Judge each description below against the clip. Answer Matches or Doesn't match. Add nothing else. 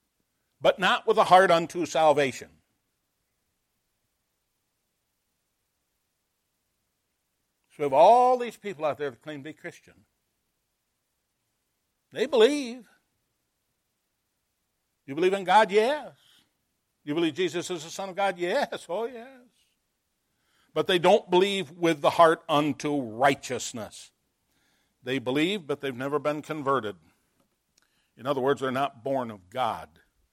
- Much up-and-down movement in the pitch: Matches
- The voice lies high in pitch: Doesn't match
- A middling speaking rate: Doesn't match